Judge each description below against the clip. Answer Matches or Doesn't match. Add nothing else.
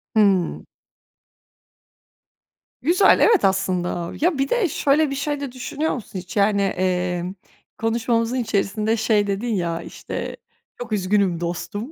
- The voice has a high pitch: Matches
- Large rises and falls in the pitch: Matches